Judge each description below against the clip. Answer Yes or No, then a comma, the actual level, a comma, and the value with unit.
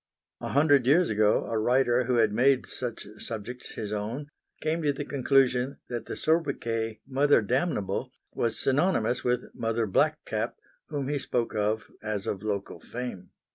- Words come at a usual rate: Yes, average, 160 wpm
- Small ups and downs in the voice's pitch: No, average, 4.1 semitones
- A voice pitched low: Yes, low, 125 Hz